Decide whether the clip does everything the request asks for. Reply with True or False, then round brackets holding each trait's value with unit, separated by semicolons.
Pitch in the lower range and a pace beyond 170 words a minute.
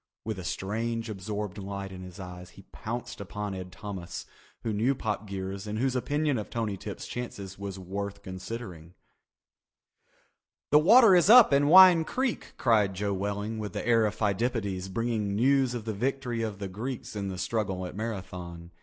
True (105 Hz; 180 wpm)